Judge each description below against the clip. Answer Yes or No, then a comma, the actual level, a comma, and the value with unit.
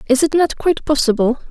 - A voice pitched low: No, very high, 280 Hz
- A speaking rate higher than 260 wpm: No, average, 200 wpm